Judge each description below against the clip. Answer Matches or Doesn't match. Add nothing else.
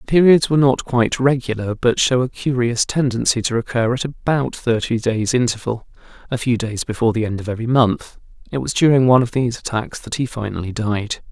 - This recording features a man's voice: Matches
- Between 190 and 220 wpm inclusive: Matches